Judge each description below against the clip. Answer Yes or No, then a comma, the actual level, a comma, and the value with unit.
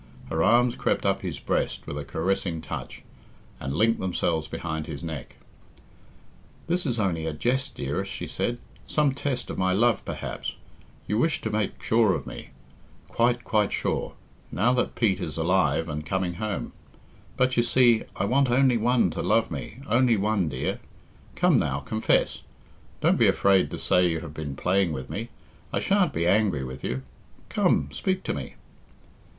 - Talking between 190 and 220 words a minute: No, average, 175 wpm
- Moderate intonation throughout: No, wide, 6.9 semitones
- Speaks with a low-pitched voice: Yes, low, 100 Hz